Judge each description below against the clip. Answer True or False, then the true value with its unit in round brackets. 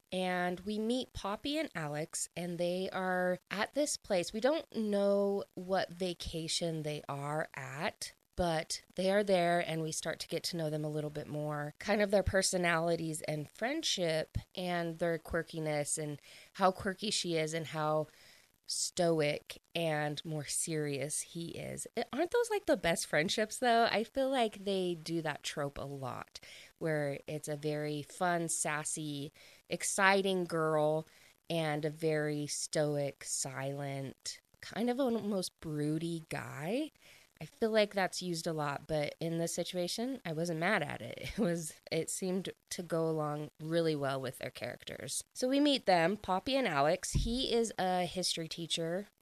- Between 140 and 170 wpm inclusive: True (160 wpm)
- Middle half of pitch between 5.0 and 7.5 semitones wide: False (4.2 semitones)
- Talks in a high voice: False (170 Hz)